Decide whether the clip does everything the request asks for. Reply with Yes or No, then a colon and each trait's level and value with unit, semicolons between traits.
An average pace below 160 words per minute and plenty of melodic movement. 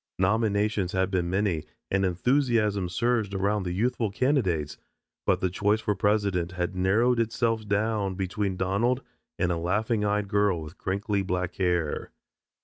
No: average, 145 wpm; average, 3.0 semitones